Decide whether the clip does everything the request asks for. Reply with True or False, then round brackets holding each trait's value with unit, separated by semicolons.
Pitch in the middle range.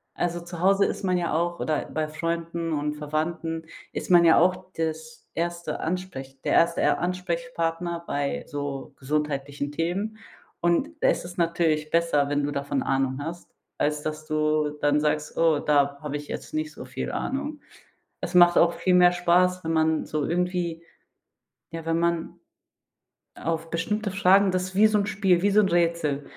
True (170 Hz)